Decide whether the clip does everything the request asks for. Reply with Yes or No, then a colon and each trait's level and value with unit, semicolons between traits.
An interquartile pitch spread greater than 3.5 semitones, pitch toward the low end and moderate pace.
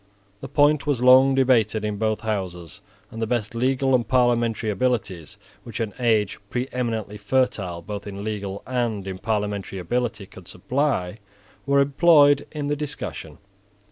Yes: average, 4.1 semitones; low, 115 Hz; average, 145 wpm